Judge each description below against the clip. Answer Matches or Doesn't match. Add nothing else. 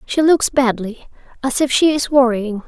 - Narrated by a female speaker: Matches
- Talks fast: Doesn't match